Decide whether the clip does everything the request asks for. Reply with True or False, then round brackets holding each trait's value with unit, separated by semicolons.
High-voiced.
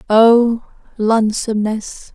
True (220 Hz)